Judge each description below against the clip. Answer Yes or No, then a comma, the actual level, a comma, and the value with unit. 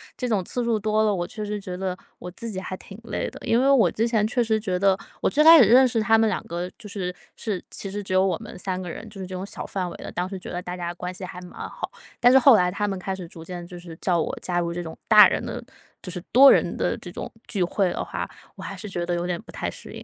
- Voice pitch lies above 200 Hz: No, high, 195 Hz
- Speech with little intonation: No, average, 3.5 semitones